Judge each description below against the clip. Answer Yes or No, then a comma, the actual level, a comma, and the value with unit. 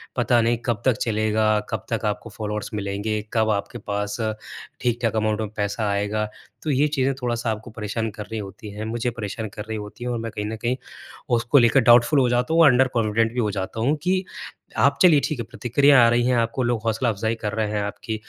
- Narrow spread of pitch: Yes, narrow, 2.3 semitones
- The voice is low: Yes, low, 115 Hz